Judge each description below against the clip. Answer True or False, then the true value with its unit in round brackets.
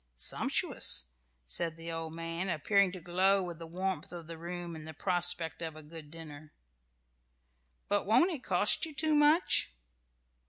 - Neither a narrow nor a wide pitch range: True (3.0 semitones)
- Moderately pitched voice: True (170 Hz)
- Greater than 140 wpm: True (160 wpm)